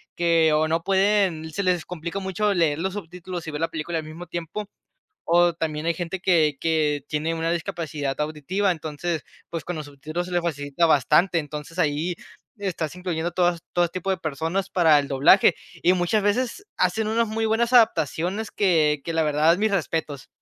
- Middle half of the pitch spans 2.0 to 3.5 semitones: Yes, average, 3.1 semitones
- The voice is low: No, medium, 170 Hz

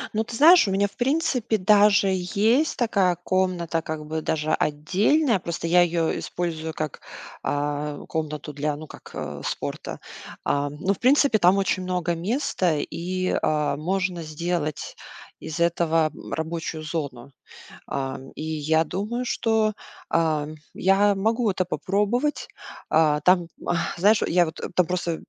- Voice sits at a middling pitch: Yes, medium, 175 Hz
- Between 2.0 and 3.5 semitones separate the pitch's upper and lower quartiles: No, average, 4.4 semitones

